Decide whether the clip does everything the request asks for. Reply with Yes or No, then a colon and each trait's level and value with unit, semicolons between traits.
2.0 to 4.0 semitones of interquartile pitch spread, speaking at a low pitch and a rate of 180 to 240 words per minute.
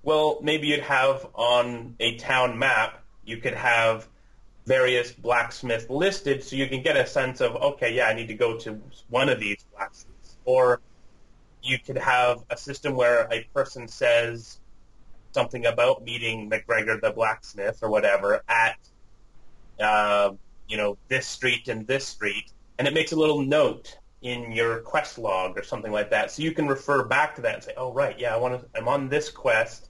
Yes: average, 3.6 semitones; low, 125 Hz; average, 185 wpm